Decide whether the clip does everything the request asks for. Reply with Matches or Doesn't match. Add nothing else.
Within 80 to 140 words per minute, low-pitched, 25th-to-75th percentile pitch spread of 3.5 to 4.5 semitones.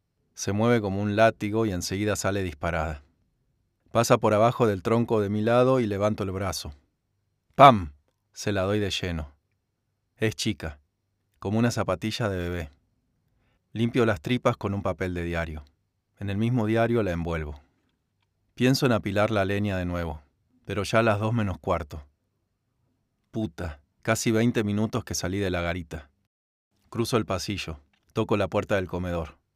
Doesn't match